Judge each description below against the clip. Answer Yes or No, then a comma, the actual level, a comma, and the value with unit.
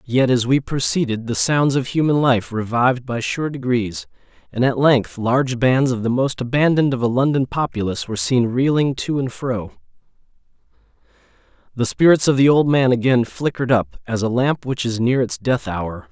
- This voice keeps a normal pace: Yes, average, 185 wpm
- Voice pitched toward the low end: Yes, low, 130 Hz